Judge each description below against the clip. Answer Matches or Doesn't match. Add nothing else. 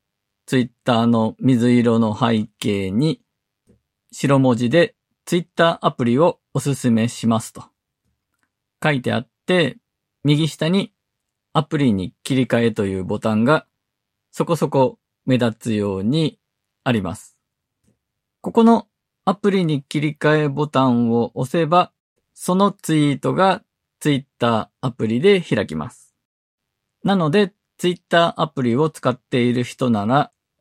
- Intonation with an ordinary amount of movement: Doesn't match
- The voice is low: Matches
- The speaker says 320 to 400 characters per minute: Doesn't match